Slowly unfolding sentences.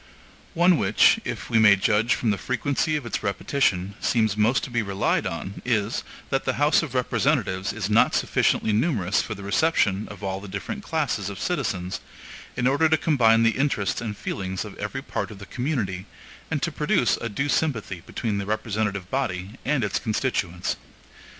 No: average, 180 wpm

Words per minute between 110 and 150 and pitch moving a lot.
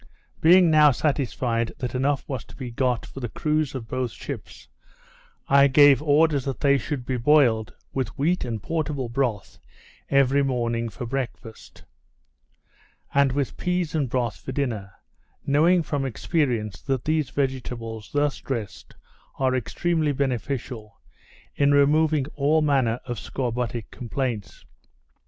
No: slow, 135 wpm; average, 3.4 semitones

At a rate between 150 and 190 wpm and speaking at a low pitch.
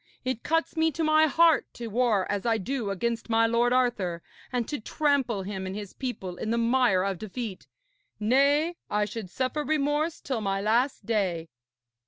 No: average, 180 wpm; high, 235 Hz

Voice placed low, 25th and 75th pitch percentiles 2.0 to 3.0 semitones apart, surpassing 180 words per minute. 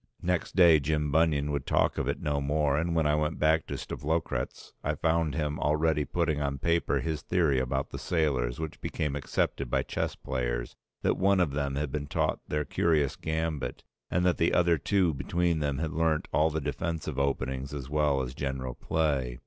Yes: very low, 75 Hz; average, 2.7 semitones; average, 195 wpm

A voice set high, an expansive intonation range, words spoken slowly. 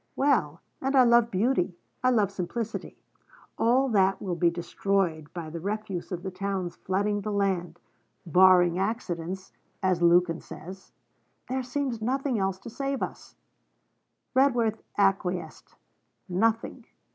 No: high, 195 Hz; average, 4.7 semitones; slow, 130 wpm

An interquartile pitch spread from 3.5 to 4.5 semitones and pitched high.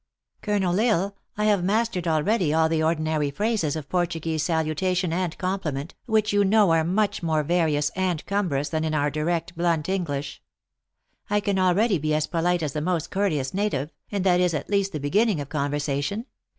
No: average, 4.2 semitones; medium, 170 Hz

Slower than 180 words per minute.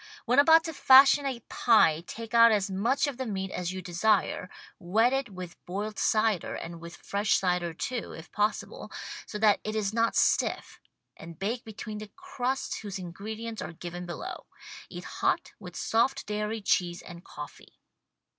Yes: average, 170 wpm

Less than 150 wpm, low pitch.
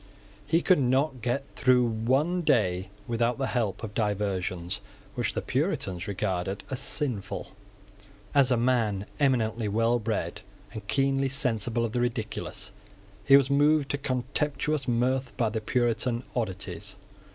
Yes: average, 140 wpm; low, 120 Hz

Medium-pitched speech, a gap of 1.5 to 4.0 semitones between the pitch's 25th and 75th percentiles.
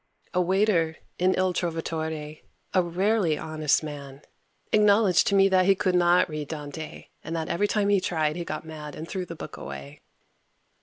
Yes: medium, 170 Hz; average, 3.3 semitones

